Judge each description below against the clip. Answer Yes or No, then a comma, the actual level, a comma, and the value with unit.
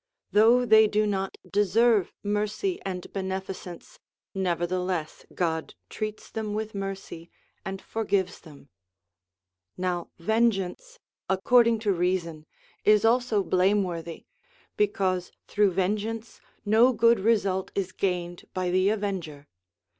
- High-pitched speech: Yes, high, 195 Hz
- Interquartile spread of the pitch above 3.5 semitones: No, average, 3.1 semitones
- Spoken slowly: Yes, slow, 110 wpm